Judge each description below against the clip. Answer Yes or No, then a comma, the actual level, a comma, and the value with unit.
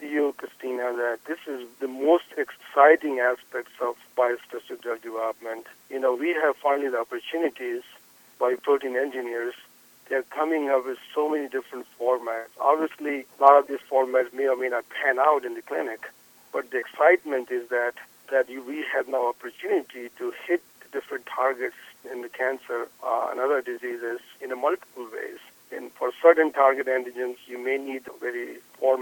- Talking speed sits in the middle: Yes, average, 170 wpm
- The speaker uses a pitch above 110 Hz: Yes, low, 135 Hz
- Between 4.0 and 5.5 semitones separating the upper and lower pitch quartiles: Yes, average, 4.3 semitones